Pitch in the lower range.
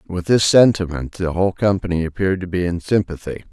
Yes: very low, 90 Hz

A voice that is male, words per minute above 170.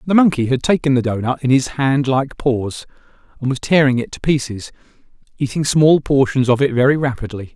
Yes: male; average, 190 wpm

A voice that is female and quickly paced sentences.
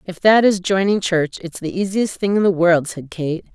Yes: female; fast, 235 wpm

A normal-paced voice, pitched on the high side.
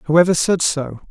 No: average, 165 wpm; medium, 165 Hz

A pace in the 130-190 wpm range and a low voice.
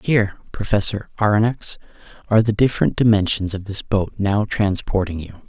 Yes: average, 140 wpm; low, 105 Hz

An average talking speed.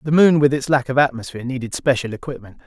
No: fast, 225 wpm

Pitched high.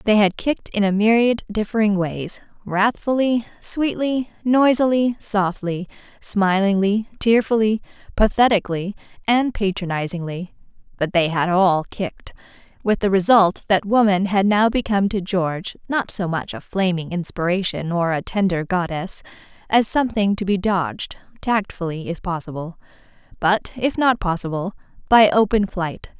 Yes: high, 200 Hz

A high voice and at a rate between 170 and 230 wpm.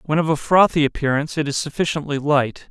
No: medium, 150 Hz; average, 200 wpm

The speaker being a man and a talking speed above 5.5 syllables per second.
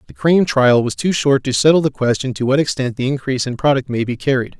Yes: male; 6.4 syllables/s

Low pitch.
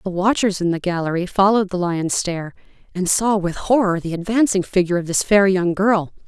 No: medium, 185 Hz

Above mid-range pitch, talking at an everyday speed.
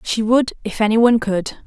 Yes: high, 230 Hz; average, 180 wpm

